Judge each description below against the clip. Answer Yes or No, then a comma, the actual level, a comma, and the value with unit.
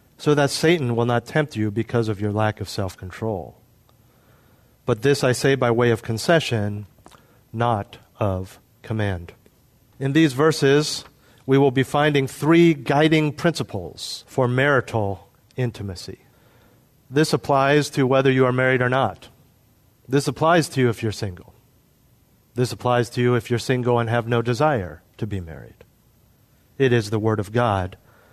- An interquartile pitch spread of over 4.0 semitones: No, average, 3.6 semitones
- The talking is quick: No, average, 155 wpm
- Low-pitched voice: Yes, low, 120 Hz